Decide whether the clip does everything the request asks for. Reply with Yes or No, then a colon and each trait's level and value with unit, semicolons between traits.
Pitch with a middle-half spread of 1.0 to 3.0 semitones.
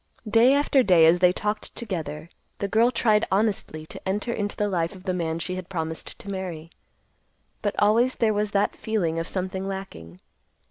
No: average, 3.9 semitones